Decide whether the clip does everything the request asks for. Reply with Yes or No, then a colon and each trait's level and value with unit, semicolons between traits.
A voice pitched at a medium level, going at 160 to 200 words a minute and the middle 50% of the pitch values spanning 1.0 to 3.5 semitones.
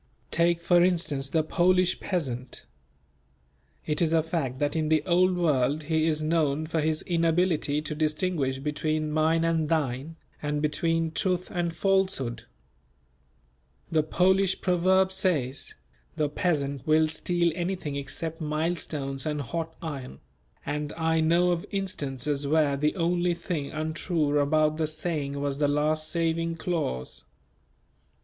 No: medium, 155 Hz; slow, 135 wpm; narrow, 2.6 semitones